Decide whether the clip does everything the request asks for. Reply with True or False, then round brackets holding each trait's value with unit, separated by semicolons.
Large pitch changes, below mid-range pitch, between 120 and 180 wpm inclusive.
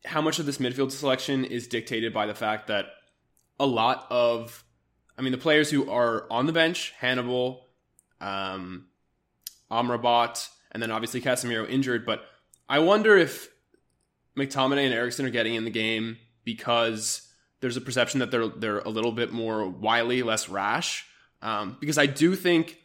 False (2.7 semitones; 120 Hz; 165 wpm)